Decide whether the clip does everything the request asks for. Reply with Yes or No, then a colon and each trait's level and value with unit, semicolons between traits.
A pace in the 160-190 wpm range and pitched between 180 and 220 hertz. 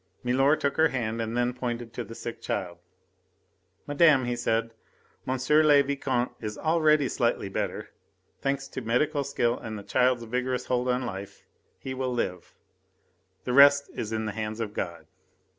No: average, 165 wpm; low, 125 Hz